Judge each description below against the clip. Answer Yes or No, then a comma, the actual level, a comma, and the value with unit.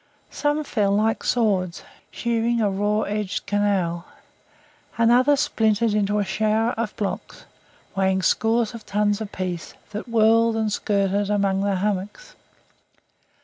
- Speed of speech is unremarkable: No, slow, 130 wpm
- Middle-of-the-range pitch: No, high, 210 Hz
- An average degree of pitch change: No, narrow, 2.3 semitones